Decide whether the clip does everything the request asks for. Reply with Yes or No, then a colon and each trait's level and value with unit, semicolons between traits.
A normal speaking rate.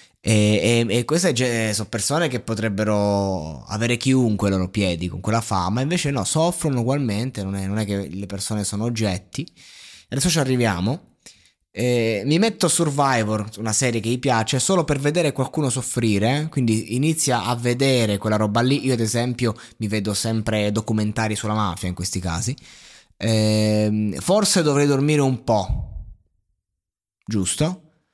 Yes: average, 160 wpm